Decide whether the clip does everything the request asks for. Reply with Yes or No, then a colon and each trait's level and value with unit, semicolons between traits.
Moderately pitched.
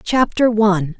No: high, 210 Hz